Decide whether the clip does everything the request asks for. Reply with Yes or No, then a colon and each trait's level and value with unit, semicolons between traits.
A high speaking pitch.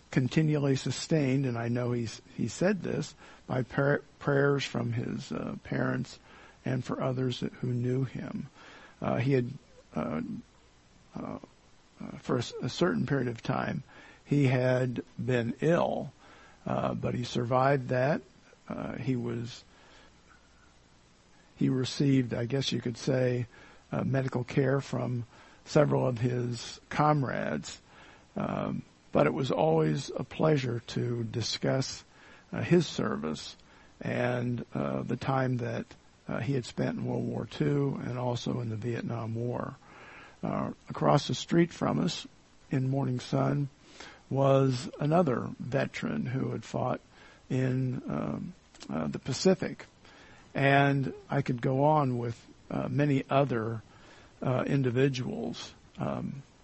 No: low, 125 Hz